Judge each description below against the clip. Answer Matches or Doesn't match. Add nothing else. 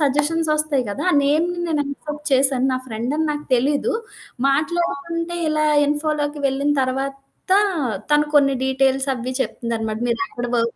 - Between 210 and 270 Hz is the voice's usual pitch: Doesn't match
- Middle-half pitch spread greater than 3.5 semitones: Doesn't match